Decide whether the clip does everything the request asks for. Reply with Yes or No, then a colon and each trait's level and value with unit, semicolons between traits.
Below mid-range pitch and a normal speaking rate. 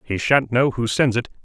No: low, 120 Hz; fast, 250 wpm